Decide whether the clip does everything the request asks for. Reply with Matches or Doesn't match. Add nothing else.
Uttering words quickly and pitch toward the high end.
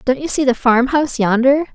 Matches